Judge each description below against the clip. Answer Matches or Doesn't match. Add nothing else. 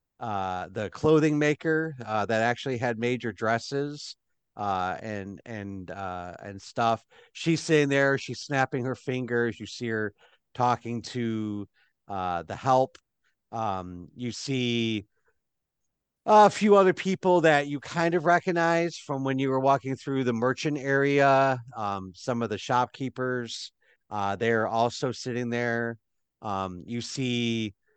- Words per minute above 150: Doesn't match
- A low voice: Matches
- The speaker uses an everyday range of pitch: Matches